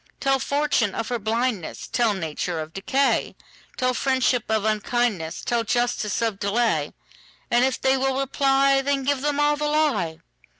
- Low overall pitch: No, high, 245 Hz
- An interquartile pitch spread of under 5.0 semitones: Yes, average, 4.3 semitones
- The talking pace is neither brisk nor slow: No, slow, 130 wpm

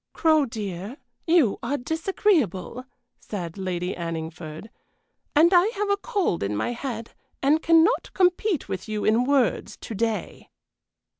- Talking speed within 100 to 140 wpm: Yes, slow, 135 wpm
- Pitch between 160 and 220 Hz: No, high, 240 Hz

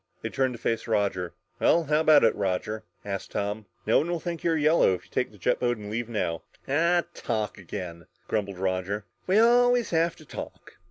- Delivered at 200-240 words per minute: Yes, fast, 205 wpm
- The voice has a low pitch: Yes, low, 115 Hz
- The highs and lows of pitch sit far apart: Yes, wide, 8.5 semitones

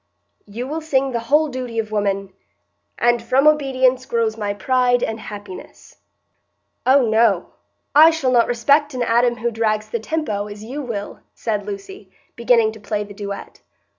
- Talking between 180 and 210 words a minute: No, average, 160 wpm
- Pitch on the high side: Yes, high, 230 Hz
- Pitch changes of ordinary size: Yes, average, 3.8 semitones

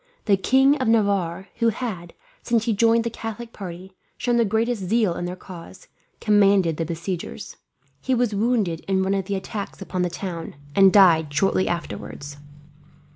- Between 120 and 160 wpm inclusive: No, average, 170 wpm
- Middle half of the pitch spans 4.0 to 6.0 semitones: Yes, average, 4.3 semitones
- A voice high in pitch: Yes, high, 195 Hz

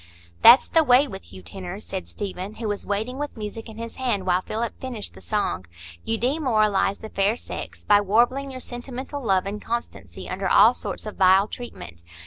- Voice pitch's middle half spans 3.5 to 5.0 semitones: Yes, average, 3.9 semitones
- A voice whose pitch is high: Yes, high, 215 Hz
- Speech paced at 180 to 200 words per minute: Yes, average, 190 wpm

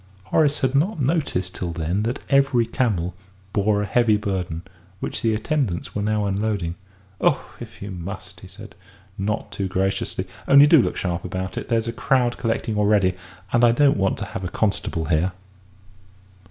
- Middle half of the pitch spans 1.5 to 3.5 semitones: No, average, 4.3 semitones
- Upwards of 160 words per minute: Yes, average, 175 wpm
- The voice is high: No, low, 105 Hz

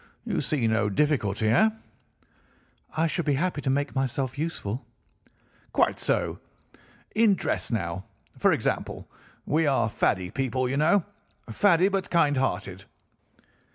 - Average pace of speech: No, slow, 125 wpm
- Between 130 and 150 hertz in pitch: Yes, low, 135 Hz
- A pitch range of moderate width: No, wide, 6.4 semitones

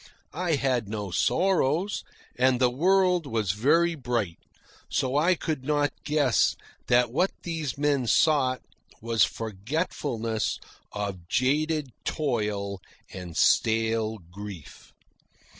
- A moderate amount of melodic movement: No, wide, 5.9 semitones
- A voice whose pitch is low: Yes, low, 125 Hz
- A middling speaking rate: No, slow, 110 wpm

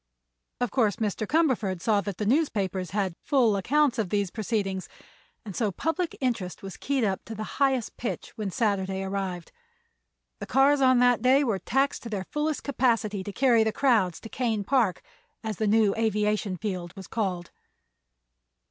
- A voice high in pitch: Yes, high, 215 Hz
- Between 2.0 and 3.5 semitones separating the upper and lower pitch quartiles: No, average, 4.6 semitones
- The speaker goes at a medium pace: Yes, average, 170 wpm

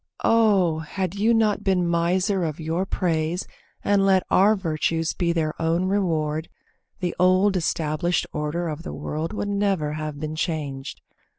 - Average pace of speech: Yes, average, 155 wpm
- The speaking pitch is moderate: Yes, medium, 170 Hz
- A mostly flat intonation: No, average, 3.6 semitones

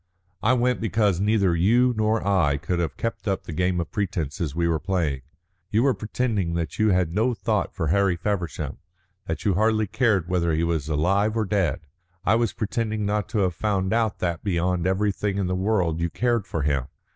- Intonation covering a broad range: No, average, 4.3 semitones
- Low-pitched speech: Yes, very low, 95 Hz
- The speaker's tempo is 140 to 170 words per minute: No, average, 200 wpm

